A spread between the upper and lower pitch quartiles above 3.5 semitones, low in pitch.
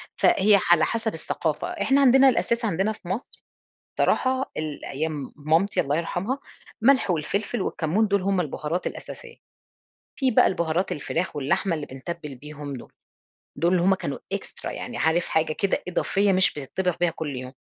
No: average, 5.2 semitones; medium, 175 Hz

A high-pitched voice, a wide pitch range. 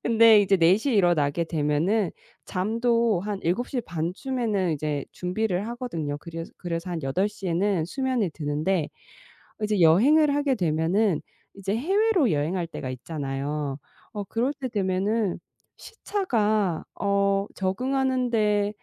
Yes: high, 195 Hz; wide, 5.7 semitones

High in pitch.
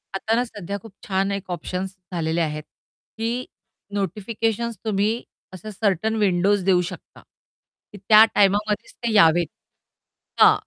Yes: high, 200 Hz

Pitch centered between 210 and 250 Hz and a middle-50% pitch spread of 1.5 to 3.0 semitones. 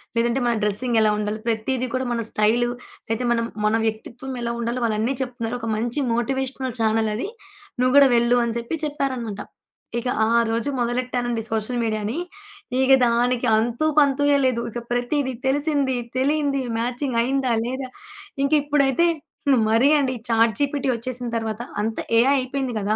Yes: high, 245 Hz; average, 2.7 semitones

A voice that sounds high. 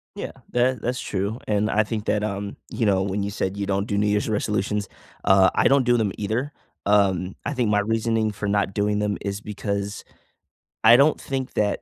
No: low, 105 Hz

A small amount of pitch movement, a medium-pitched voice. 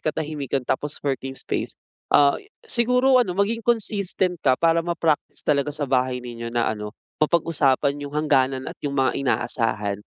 No: average, 4.7 semitones; medium, 145 Hz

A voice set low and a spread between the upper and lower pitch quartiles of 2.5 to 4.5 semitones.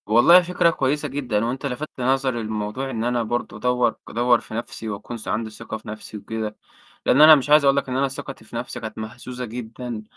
Yes: low, 120 Hz; average, 3.4 semitones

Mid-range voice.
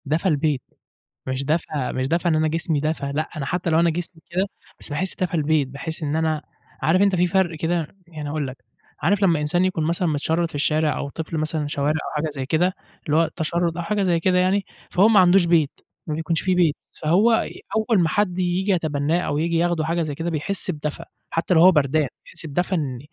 Yes: medium, 165 Hz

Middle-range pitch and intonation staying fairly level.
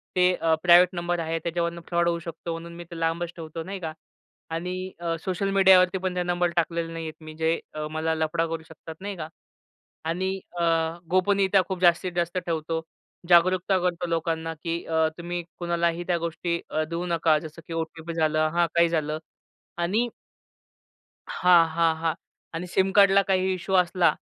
Yes: medium, 170 Hz; narrow, 1.7 semitones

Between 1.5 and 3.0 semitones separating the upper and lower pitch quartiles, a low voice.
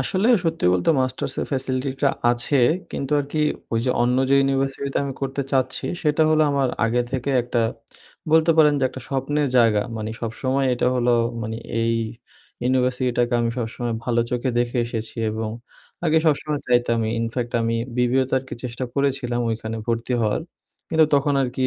Yes: average, 2.7 semitones; low, 130 Hz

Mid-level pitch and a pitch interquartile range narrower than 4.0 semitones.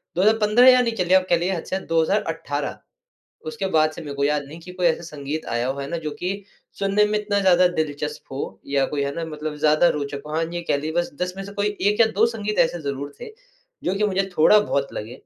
No: medium, 165 Hz; average, 4.9 semitones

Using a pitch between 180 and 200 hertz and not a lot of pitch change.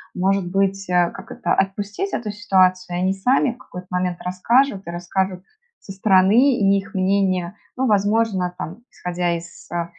Yes: high, 190 Hz; narrow, 2.2 semitones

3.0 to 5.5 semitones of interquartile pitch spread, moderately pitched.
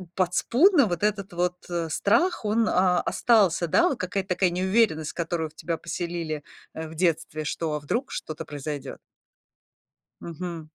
Yes: average, 3.8 semitones; medium, 175 Hz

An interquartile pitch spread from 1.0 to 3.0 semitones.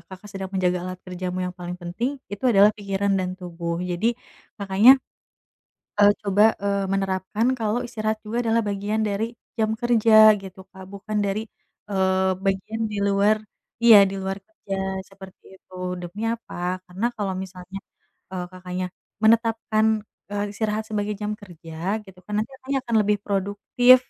Yes: narrow, 2.4 semitones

